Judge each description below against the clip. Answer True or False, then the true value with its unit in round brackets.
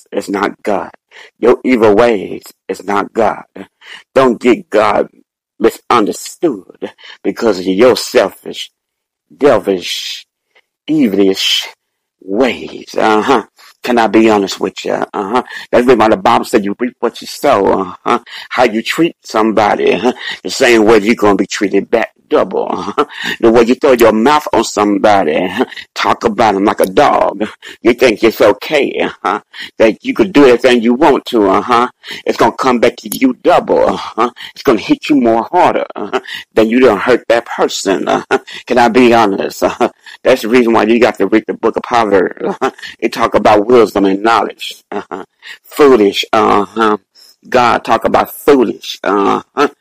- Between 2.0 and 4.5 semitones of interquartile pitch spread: False (5.6 semitones)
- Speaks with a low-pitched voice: True (115 Hz)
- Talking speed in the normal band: True (170 wpm)